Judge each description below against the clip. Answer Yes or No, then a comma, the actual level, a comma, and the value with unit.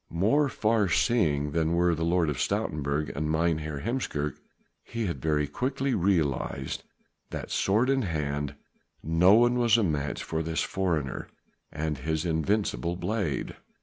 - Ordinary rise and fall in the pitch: No, wide, 5.9 semitones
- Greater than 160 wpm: No, average, 145 wpm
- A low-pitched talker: Yes, very low, 85 Hz